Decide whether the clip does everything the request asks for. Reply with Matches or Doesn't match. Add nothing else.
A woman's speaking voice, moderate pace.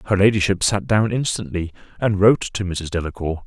Doesn't match